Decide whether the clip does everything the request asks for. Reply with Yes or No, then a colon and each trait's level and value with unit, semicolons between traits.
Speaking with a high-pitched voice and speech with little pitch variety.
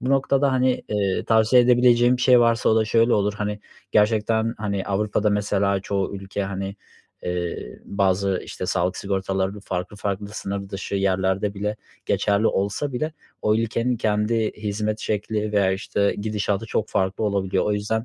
No: low, 105 Hz; narrow, 2.2 semitones